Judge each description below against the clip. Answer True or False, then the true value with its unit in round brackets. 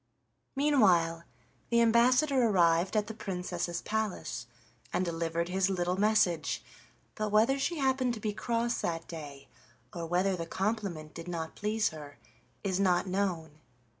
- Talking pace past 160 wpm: False (140 wpm)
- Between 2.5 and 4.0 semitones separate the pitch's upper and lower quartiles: False (4.6 semitones)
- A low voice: False (190 Hz)